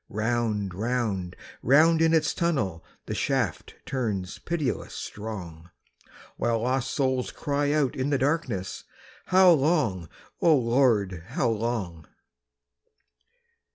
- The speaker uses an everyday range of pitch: No, wide, 6.2 semitones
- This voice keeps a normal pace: No, slow, 110 wpm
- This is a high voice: No, low, 120 Hz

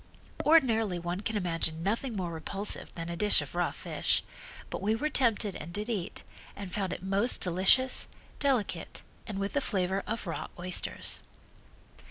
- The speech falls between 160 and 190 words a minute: Yes, average, 165 wpm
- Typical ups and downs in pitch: Yes, average, 4.0 semitones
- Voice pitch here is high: Yes, high, 200 Hz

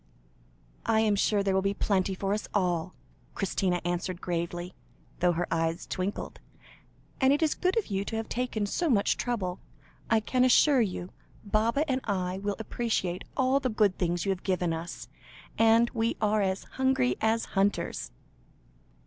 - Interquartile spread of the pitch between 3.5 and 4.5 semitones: Yes, average, 4.0 semitones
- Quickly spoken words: No, average, 165 wpm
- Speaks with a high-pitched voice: Yes, high, 200 Hz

